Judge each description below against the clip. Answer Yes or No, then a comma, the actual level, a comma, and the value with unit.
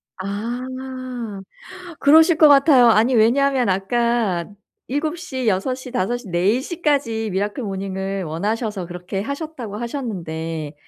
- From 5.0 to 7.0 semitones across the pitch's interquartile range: Yes, wide, 5.4 semitones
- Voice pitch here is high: Yes, high, 225 Hz